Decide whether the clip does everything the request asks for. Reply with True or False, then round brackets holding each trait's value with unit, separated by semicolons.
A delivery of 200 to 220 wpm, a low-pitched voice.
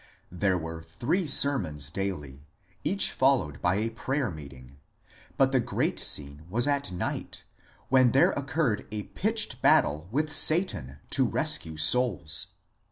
False (135 wpm; 105 Hz)